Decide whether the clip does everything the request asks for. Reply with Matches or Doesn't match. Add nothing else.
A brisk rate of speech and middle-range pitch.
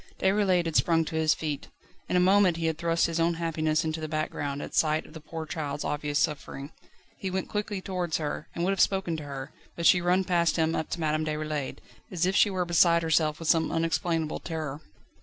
Matches